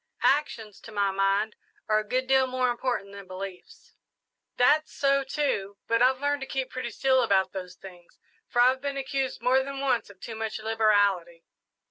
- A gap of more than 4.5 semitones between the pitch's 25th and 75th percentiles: Yes, average, 4.9 semitones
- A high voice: Yes, high, 230 Hz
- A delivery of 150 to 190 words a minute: Yes, average, 180 wpm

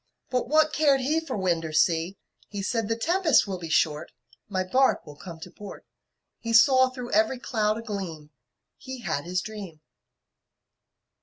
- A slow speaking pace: No, average, 170 wpm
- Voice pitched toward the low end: No, high, 210 Hz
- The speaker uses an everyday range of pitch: No, wide, 6.8 semitones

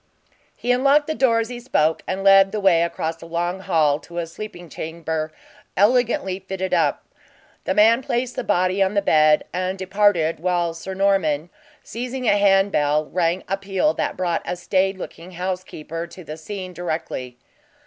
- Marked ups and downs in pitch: No, average, 3.4 semitones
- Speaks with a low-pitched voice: No, medium, 185 Hz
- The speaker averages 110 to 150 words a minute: No, average, 170 wpm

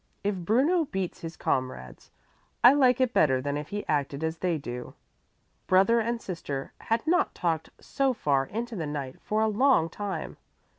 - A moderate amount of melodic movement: No, wide, 8.0 semitones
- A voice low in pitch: No, medium, 185 Hz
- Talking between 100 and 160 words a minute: No, average, 170 wpm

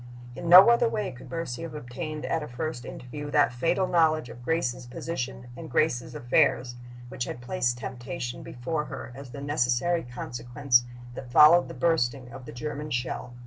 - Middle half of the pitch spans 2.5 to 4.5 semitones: No, average, 4.9 semitones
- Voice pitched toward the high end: No, low, 135 Hz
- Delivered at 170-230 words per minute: Yes, average, 175 wpm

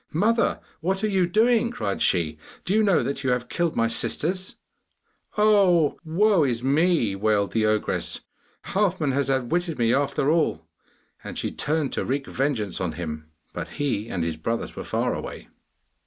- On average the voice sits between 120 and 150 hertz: Yes, medium, 140 Hz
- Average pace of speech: Yes, average, 170 wpm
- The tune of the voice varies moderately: No, wide, 8.2 semitones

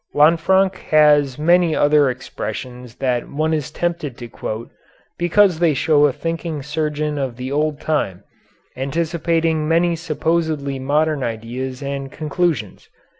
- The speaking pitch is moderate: Yes, medium, 150 Hz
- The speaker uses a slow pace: Yes, slow, 125 wpm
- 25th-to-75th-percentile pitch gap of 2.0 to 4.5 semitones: Yes, average, 3.6 semitones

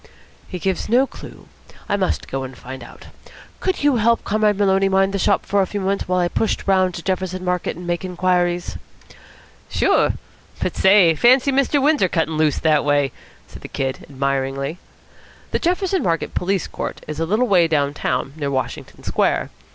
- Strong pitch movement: No, average, 4.7 semitones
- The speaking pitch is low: No, medium, 180 Hz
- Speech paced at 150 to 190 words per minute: Yes, average, 180 wpm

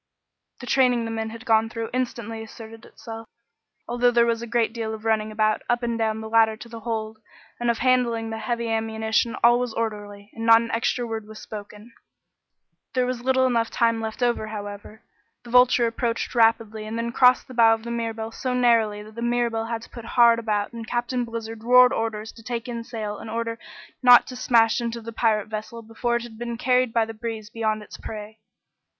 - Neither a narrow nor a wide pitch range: No, narrow, 1.4 semitones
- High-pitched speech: Yes, high, 230 Hz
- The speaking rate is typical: No, fast, 215 wpm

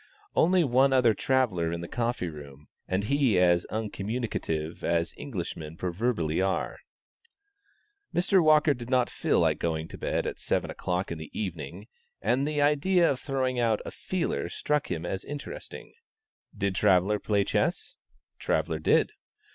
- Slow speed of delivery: No, average, 150 wpm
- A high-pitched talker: No, low, 105 Hz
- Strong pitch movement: Yes, wide, 7.6 semitones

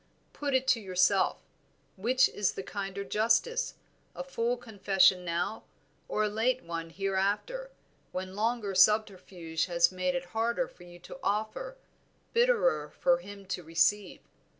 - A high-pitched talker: Yes, high, 200 Hz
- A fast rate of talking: No, average, 140 wpm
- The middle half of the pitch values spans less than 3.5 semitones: No, average, 4.5 semitones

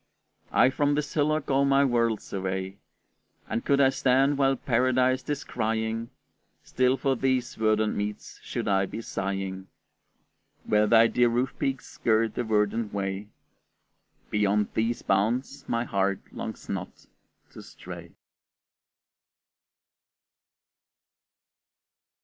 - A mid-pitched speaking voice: No, low, 115 Hz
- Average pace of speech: No, slow, 115 wpm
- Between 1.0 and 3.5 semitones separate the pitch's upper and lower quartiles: No, average, 4.2 semitones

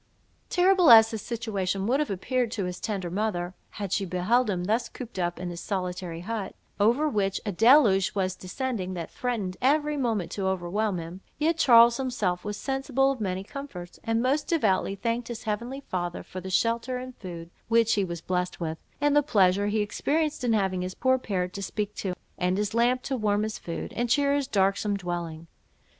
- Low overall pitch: No, high, 210 Hz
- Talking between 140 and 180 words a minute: No, average, 195 wpm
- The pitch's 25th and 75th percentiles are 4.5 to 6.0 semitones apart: Yes, average, 5.1 semitones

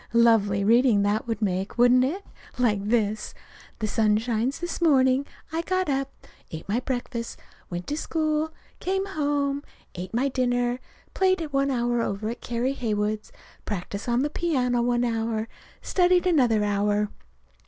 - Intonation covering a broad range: No, average, 4.6 semitones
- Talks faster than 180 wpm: No, average, 150 wpm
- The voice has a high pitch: Yes, high, 245 Hz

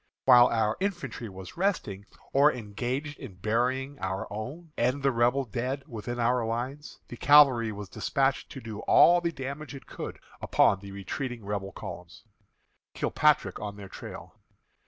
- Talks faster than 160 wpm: No, average, 155 wpm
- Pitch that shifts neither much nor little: Yes, average, 4.6 semitones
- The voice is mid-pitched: No, low, 120 Hz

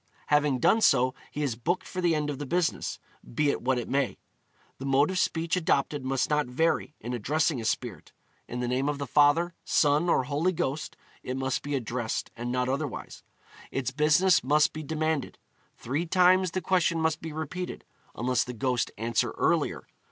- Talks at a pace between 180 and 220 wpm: Yes, average, 190 wpm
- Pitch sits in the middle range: Yes, medium, 145 Hz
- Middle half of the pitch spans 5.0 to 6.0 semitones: No, average, 4.0 semitones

